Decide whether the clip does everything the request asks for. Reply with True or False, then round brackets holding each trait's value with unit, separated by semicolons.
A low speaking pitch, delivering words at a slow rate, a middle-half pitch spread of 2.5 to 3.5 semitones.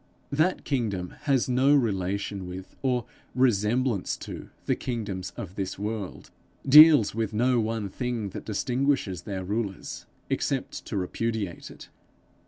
False (110 Hz; 130 wpm; 4.5 semitones)